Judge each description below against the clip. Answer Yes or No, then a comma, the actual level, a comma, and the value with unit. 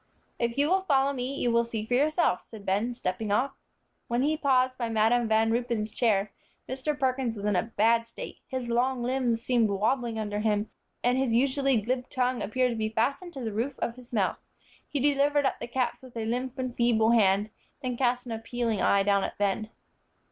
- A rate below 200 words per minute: No, fast, 205 wpm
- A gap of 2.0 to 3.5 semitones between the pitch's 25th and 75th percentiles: Yes, average, 2.8 semitones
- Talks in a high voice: Yes, high, 240 Hz